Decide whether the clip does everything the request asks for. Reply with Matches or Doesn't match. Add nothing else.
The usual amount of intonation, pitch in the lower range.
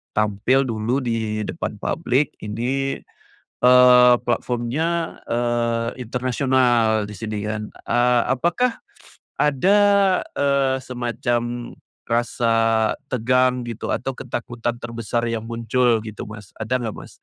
Doesn't match